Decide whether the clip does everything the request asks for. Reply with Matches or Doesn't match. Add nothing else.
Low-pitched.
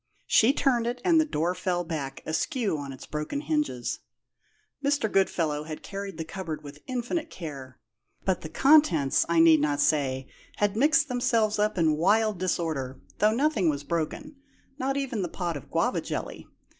Doesn't match